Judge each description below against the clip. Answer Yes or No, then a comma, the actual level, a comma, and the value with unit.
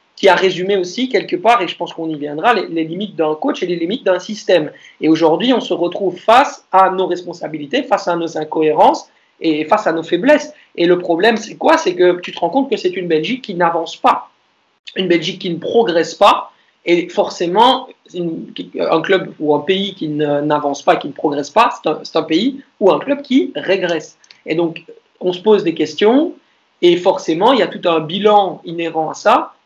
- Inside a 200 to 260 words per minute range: Yes, average, 215 wpm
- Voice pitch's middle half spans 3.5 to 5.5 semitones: Yes, average, 4.5 semitones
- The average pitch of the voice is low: No, medium, 180 Hz